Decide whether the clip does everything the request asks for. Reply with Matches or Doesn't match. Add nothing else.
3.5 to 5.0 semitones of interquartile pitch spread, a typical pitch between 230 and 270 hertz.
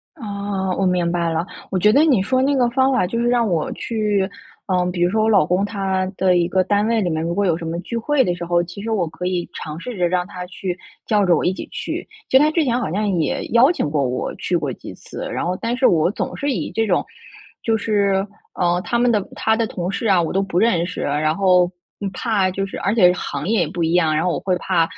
Doesn't match